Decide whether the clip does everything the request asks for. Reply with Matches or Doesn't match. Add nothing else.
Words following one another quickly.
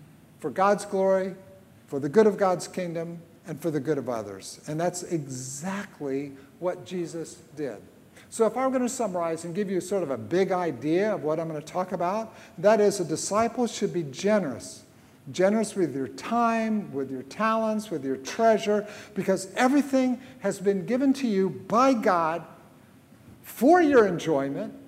Doesn't match